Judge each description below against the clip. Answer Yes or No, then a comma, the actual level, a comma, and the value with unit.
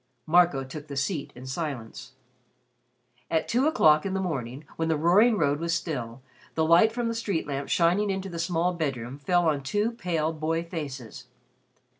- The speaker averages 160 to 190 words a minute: Yes, average, 175 wpm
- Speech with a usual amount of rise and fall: Yes, average, 4.3 semitones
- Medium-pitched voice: Yes, medium, 160 Hz